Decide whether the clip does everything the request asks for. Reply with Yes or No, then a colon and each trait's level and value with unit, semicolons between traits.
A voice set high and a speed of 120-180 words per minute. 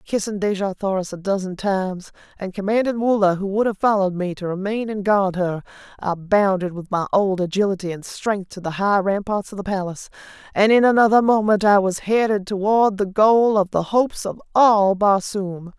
No: high, 200 Hz; average, 190 wpm